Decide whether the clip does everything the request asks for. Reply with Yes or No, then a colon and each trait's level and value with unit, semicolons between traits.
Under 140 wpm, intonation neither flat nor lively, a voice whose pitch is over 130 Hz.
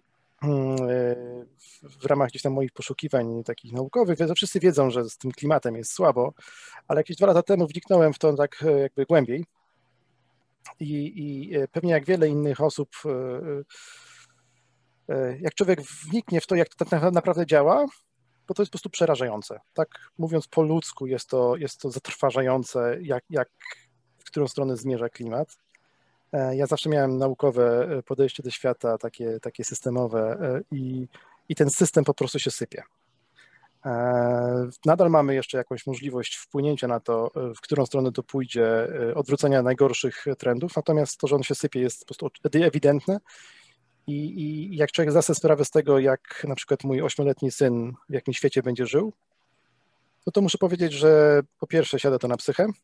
No: fast, 160 wpm; average, 3.8 semitones; medium, 140 Hz